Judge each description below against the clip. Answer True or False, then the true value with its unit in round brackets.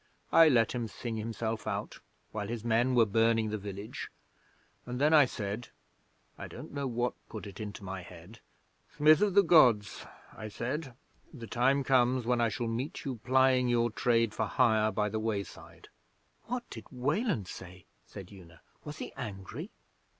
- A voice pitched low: True (115 Hz)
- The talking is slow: False (170 wpm)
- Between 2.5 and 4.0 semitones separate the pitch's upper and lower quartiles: True (3.5 semitones)